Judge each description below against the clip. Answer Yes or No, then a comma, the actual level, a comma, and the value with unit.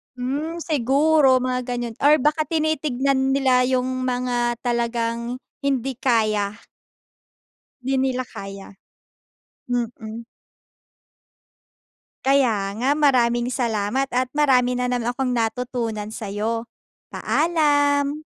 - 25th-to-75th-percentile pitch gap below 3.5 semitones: Yes, average, 2.8 semitones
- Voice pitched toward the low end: No, very high, 250 Hz